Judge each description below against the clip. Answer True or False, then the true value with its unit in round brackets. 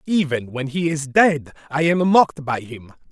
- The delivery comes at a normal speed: True (195 wpm)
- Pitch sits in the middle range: True (150 Hz)